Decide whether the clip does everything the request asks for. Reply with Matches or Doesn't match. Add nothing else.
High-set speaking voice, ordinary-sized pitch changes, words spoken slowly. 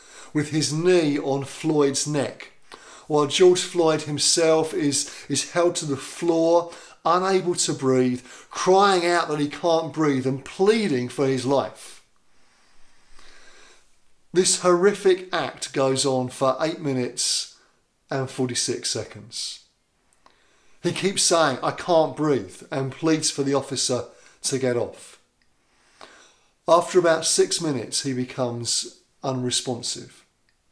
Doesn't match